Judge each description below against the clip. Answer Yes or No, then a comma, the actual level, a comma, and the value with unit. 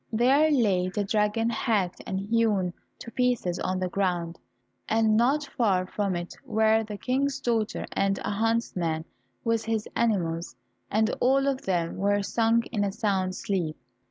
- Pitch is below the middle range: No, high, 210 Hz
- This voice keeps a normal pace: Yes, average, 155 wpm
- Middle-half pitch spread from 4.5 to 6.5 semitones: No, average, 3.7 semitones